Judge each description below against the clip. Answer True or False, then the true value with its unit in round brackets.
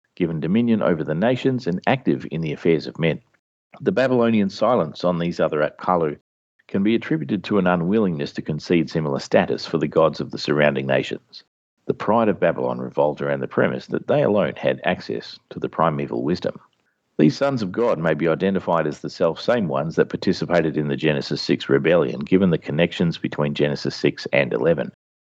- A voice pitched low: True (80 Hz)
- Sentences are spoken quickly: False (185 wpm)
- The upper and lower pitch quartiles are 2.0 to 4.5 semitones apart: False (5.3 semitones)